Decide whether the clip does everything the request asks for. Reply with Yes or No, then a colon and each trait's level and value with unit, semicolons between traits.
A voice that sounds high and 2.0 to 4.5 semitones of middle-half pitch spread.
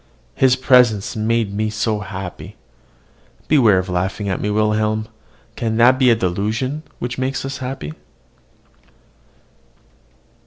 No: low, 110 Hz; average, 3.8 semitones